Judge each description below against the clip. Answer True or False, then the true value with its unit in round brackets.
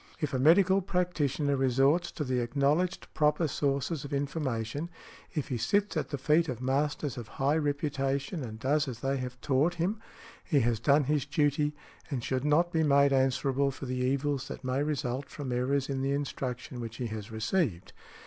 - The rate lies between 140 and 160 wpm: False (175 wpm)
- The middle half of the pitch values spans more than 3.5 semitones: False (2.8 semitones)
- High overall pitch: False (140 Hz)